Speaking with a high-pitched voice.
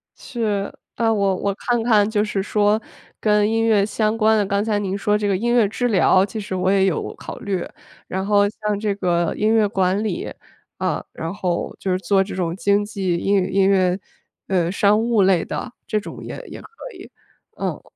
Yes: high, 205 Hz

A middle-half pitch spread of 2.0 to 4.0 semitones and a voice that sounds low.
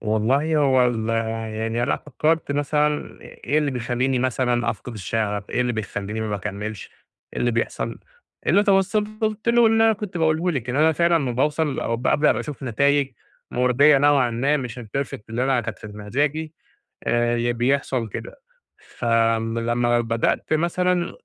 No: average, 4.8 semitones; low, 125 Hz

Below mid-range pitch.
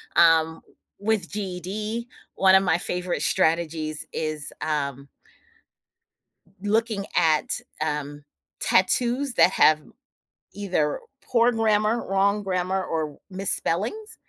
No: medium, 185 Hz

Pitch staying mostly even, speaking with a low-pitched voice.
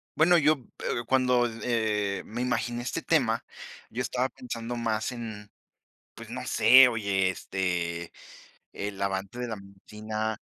No: average, 3.7 semitones; low, 110 Hz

